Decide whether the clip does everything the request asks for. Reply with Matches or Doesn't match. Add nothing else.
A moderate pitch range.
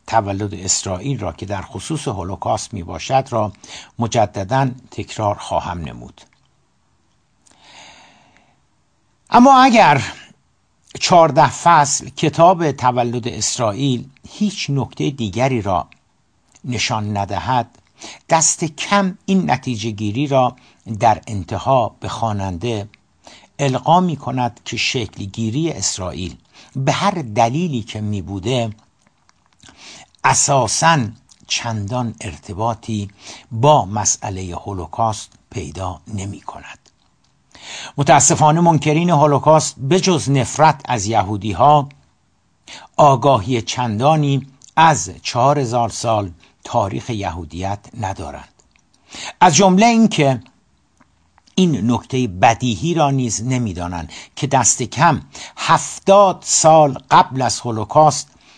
Doesn't match